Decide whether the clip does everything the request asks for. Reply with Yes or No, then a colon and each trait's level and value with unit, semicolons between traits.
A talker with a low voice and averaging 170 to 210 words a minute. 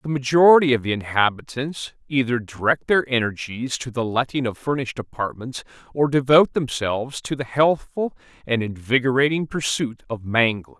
No: low, 130 Hz; average, 145 wpm